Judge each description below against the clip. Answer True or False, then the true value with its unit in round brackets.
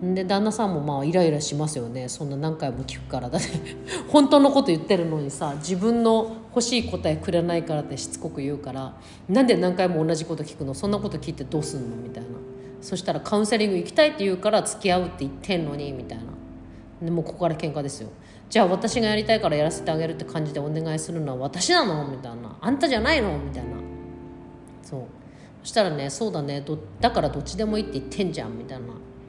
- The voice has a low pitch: False (155 Hz)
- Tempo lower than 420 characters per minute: False (465 characters per minute)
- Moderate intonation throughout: False (6.4 semitones)